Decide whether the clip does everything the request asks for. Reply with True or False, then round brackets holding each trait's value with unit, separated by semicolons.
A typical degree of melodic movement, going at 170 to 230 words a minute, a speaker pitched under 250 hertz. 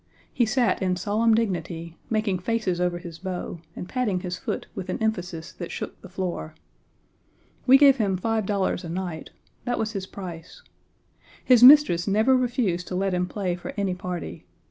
True (3.8 semitones; 175 wpm; 190 Hz)